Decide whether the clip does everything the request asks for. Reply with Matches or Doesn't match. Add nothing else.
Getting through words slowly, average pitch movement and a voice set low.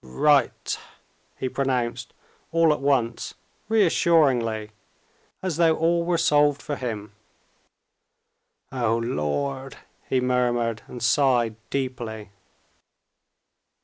Matches